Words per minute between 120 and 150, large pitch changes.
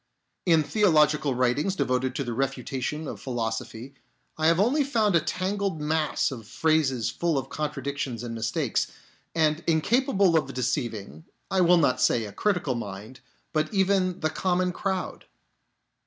Yes: average, 145 wpm; wide, 6.0 semitones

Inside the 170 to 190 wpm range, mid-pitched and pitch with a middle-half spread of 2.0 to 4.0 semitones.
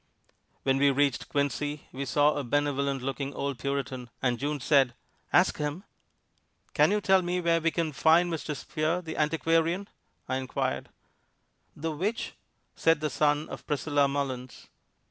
No: average, 150 wpm; medium, 145 Hz; average, 2.9 semitones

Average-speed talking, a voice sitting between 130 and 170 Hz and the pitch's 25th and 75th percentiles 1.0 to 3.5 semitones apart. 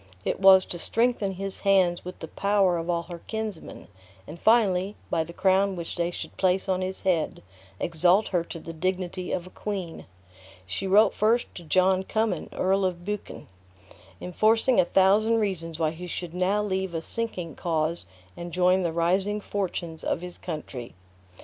No: average, 175 wpm; medium, 185 Hz; narrow, 2.5 semitones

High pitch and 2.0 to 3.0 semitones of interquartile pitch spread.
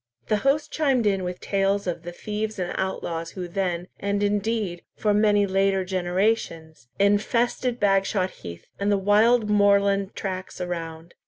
Yes: high, 195 Hz; narrow, 2.6 semitones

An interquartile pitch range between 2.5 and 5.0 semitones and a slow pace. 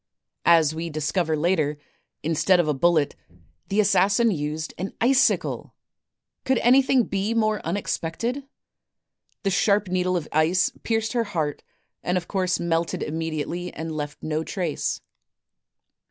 Yes: average, 4.3 semitones; slow, 130 wpm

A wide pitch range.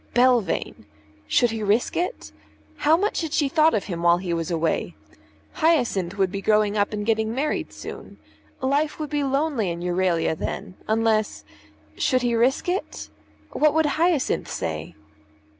Yes: wide, 7.8 semitones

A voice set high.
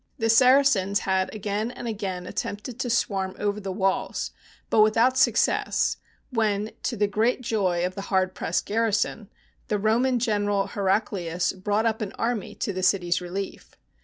Yes: high, 205 Hz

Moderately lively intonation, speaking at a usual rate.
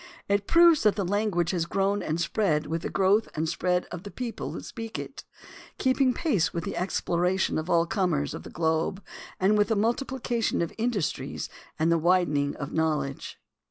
Yes: average, 4.5 semitones; average, 190 wpm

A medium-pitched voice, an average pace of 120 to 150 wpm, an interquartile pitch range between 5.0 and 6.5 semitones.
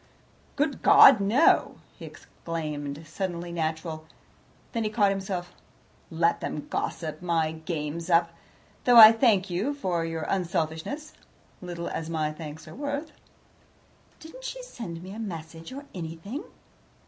Yes: medium, 175 Hz; slow, 135 wpm; wide, 5.4 semitones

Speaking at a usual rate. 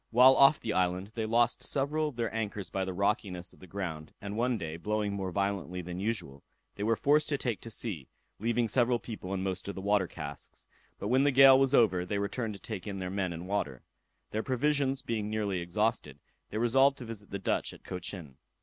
No: fast, 220 wpm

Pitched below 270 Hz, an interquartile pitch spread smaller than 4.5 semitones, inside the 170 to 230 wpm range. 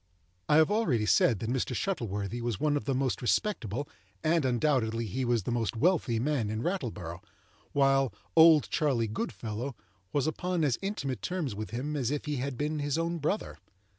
No: low, 135 Hz; average, 5.0 semitones; average, 180 wpm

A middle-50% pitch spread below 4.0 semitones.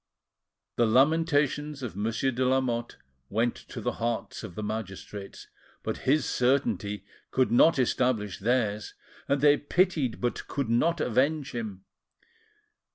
No: average, 4.3 semitones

